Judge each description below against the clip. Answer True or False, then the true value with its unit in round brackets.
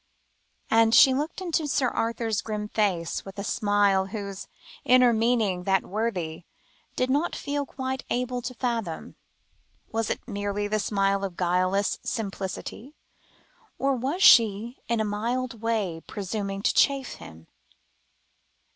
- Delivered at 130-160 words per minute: True (135 wpm)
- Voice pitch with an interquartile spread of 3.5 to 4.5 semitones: True (4.0 semitones)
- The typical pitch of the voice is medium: False (220 Hz)